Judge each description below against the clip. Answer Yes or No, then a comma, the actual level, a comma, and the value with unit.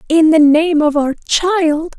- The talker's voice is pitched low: No, very high, 315 Hz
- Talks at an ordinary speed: Yes, average, 180 wpm